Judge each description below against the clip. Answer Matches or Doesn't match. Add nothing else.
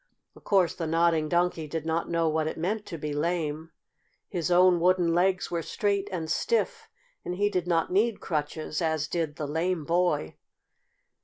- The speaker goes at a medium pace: Matches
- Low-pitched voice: Doesn't match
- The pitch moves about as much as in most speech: Doesn't match